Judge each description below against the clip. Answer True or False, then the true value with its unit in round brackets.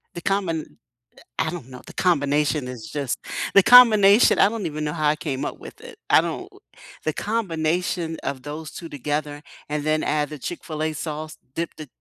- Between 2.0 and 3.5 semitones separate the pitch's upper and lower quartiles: True (2.8 semitones)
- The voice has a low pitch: False (155 Hz)